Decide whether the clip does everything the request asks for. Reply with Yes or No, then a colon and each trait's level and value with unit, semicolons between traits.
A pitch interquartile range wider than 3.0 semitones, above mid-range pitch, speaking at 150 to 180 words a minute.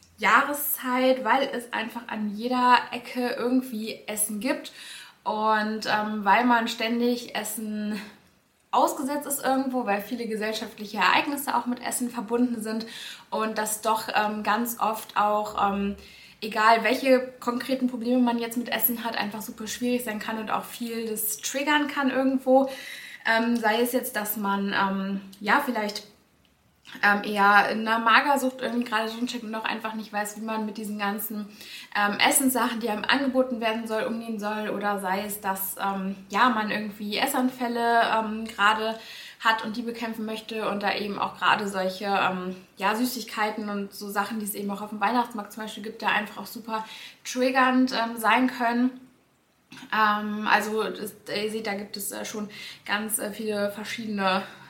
No: narrow, 2.6 semitones; high, 220 Hz; average, 165 wpm